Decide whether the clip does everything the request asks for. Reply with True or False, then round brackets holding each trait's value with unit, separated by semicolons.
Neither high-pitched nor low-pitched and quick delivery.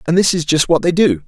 True (165 Hz; 330 wpm)